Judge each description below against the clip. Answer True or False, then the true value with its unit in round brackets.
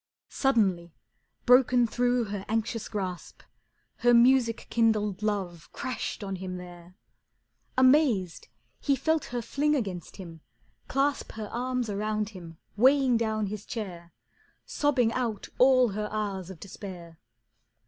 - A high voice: True (215 Hz)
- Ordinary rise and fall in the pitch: True (4.7 semitones)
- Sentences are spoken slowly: True (125 wpm)